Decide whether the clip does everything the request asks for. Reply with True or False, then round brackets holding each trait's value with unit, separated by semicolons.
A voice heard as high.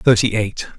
False (110 Hz)